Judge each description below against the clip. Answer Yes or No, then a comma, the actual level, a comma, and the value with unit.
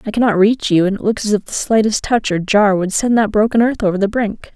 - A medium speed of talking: No, fast, 275 wpm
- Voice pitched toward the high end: Yes, high, 210 Hz